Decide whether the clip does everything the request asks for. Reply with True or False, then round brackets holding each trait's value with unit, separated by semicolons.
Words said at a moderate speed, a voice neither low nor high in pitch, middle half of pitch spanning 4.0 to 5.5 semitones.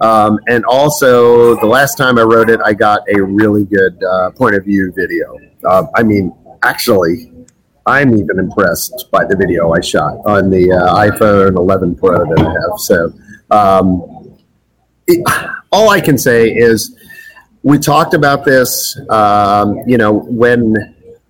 False (160 wpm; 110 Hz; 4.3 semitones)